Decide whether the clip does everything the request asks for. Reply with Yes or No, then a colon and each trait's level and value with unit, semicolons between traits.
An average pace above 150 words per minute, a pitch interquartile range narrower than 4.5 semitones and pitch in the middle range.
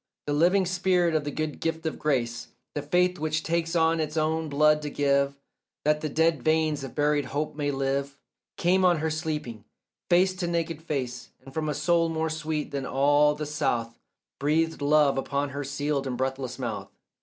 Yes: average, 185 wpm; narrow, 2.5 semitones; medium, 150 Hz